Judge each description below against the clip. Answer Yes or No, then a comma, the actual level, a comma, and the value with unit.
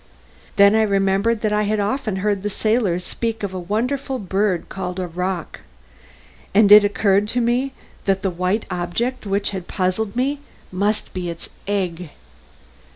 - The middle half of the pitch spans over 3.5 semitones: No, average, 2.8 semitones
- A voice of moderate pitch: No, high, 200 Hz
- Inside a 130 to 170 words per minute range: Yes, average, 165 wpm